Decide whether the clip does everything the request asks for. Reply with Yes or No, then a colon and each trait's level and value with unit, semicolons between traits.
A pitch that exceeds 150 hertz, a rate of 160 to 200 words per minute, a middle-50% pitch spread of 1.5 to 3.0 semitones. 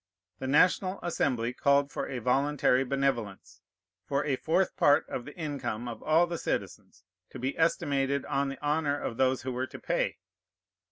No: medium, 140 Hz; average, 170 wpm; average, 2.7 semitones